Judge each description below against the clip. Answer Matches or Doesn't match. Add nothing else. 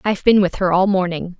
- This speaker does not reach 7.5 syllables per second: Matches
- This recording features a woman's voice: Matches